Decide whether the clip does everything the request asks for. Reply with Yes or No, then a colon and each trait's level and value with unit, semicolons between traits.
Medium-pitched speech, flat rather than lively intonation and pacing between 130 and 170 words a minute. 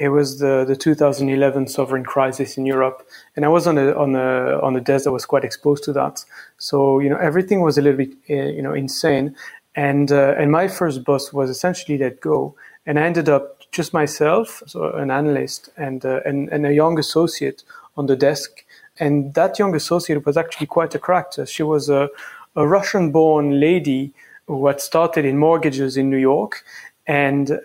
No: medium, 145 Hz; narrow, 2.3 semitones; average, 200 wpm